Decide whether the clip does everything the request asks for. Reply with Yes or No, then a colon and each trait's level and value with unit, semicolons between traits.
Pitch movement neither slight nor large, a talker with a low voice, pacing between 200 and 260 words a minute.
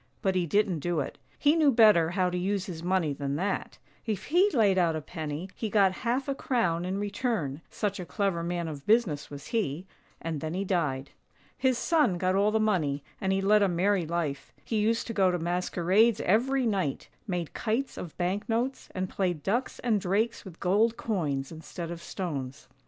No: average, 4.4 semitones; high, 190 Hz; fast, 205 wpm